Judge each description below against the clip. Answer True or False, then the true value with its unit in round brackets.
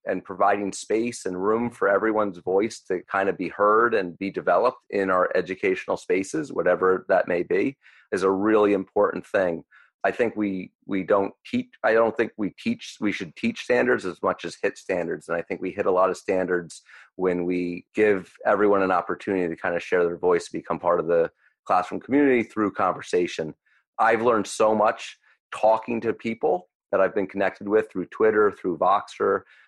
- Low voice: True (110 Hz)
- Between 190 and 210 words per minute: True (195 wpm)